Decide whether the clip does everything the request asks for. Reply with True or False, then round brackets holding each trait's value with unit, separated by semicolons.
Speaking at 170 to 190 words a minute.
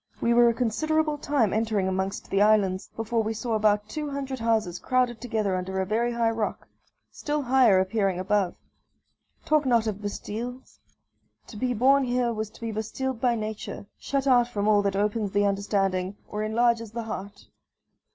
True (175 wpm)